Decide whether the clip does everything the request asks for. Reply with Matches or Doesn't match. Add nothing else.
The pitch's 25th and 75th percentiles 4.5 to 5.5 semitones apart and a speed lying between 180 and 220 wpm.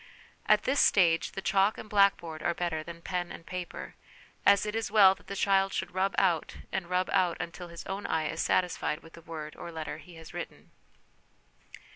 Doesn't match